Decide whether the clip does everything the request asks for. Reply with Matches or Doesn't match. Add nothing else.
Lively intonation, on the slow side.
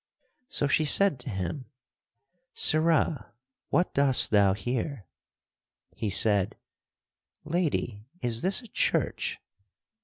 Matches